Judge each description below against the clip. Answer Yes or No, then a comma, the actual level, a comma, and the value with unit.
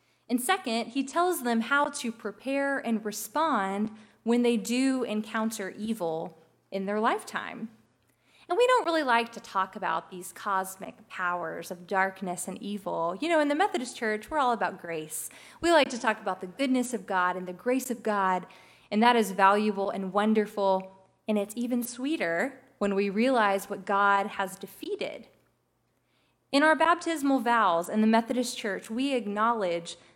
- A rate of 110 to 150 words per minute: No, average, 165 wpm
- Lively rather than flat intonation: No, average, 4.6 semitones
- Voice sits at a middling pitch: No, high, 215 Hz